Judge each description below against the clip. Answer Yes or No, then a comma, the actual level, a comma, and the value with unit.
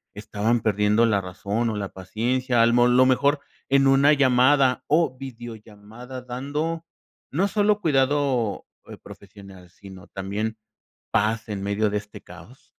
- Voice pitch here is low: Yes, low, 120 Hz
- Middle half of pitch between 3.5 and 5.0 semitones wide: Yes, average, 4.6 semitones